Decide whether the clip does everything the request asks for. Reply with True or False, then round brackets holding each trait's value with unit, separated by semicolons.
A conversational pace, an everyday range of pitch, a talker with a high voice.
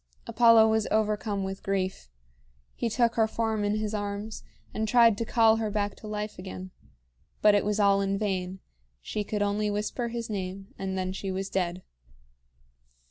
False (175 wpm; 2.1 semitones; 210 Hz)